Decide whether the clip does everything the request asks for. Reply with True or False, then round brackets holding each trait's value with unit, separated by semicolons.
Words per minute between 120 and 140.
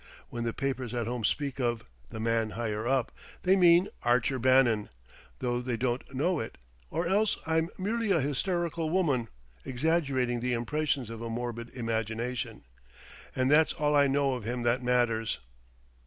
False (160 wpm)